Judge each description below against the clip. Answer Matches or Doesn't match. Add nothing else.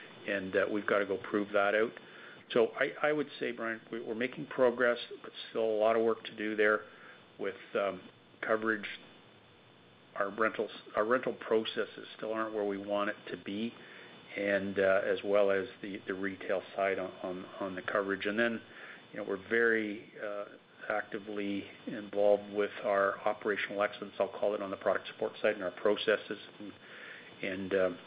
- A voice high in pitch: Doesn't match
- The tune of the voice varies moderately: Doesn't match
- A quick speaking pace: Doesn't match